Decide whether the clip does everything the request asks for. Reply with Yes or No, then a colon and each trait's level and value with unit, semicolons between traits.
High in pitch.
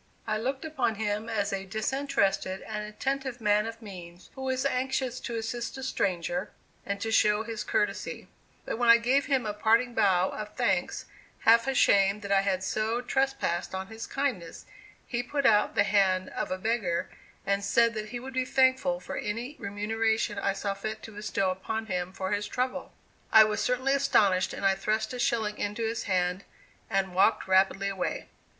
Yes: high, 215 Hz